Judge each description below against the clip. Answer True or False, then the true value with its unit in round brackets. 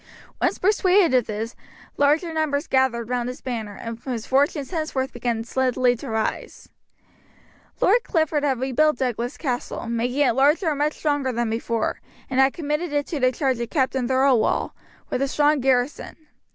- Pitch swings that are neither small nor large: True (3.5 semitones)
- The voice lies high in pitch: True (265 Hz)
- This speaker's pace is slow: False (165 wpm)